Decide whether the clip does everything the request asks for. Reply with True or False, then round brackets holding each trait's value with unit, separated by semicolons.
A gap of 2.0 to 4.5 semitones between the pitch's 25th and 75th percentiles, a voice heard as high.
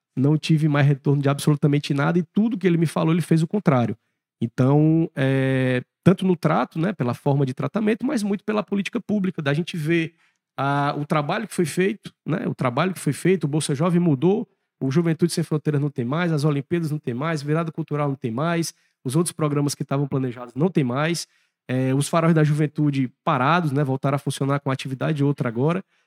False (3.5 semitones; 155 Hz)